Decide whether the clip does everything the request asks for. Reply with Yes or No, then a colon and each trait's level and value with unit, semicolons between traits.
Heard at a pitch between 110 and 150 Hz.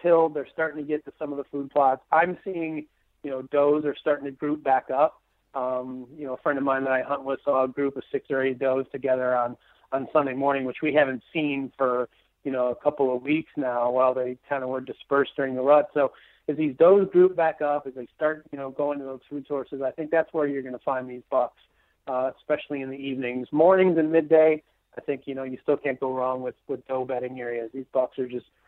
Yes: medium, 140 Hz